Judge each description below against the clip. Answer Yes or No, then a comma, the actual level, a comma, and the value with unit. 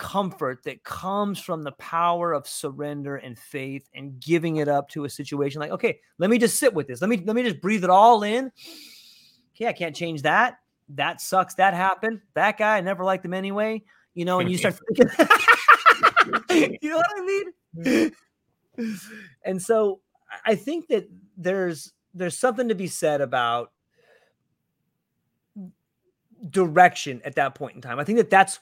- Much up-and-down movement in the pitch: Yes, wide, 6.3 semitones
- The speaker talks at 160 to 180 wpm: Yes, average, 175 wpm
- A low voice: No, medium, 185 Hz